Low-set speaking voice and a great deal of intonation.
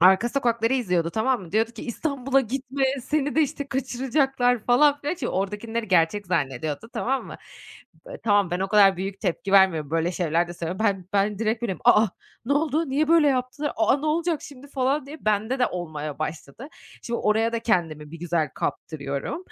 No: high, 225 Hz; wide, 7.0 semitones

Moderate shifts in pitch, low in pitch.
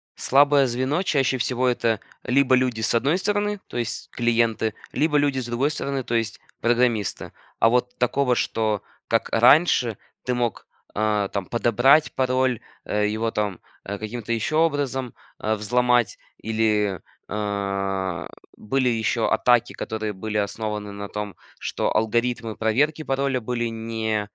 Yes: average, 3.3 semitones; low, 120 Hz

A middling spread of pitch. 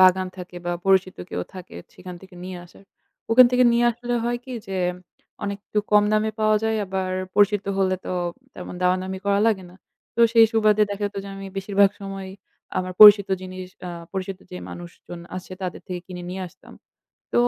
No: narrow, 2.2 semitones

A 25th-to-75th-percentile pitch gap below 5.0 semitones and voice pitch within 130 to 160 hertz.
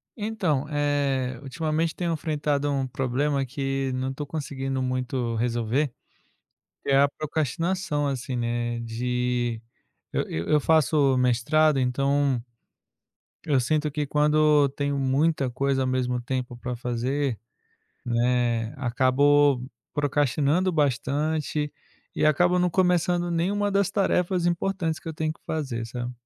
Yes: average, 3.5 semitones; medium, 140 Hz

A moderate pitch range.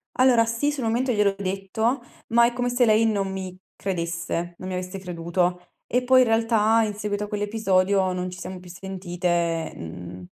Yes: average, 3.9 semitones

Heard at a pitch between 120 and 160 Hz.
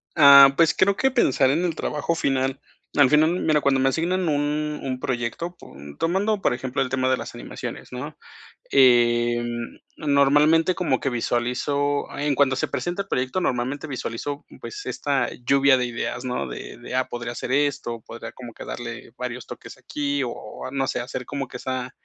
Yes: low, 135 Hz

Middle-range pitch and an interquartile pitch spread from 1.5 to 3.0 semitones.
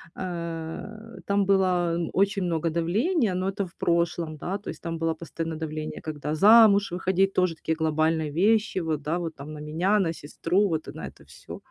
No: medium, 170 Hz; average, 3.4 semitones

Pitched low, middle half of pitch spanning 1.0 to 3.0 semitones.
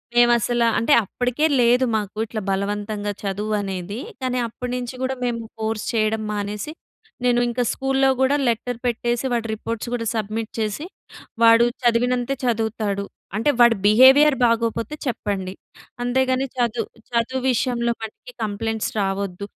No: high, 230 Hz; narrow, 2.6 semitones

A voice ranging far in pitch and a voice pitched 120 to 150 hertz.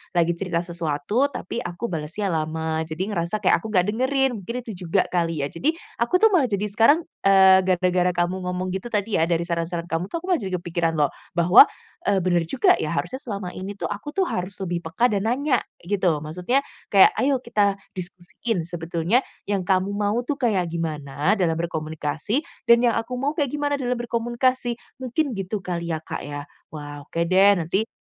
No: wide, 5.7 semitones; medium, 185 Hz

